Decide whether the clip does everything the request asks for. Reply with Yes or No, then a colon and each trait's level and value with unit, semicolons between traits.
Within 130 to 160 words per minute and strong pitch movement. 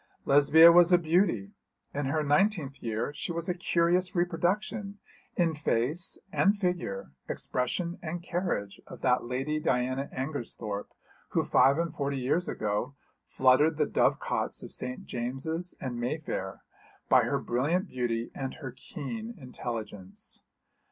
Yes: average, 140 wpm; wide, 5.7 semitones